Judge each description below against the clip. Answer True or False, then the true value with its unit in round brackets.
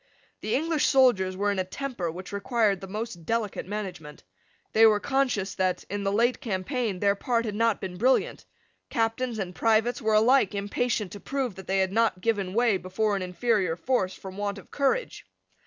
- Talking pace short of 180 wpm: False (190 wpm)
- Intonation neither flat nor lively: True (3.8 semitones)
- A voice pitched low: False (210 Hz)